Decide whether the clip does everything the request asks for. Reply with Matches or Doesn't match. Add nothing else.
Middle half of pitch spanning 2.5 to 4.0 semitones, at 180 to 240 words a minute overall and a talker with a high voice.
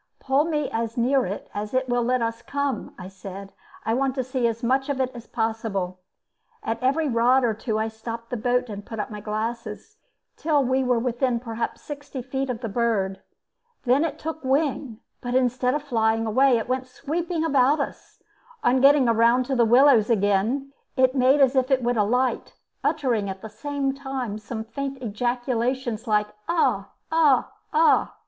Matches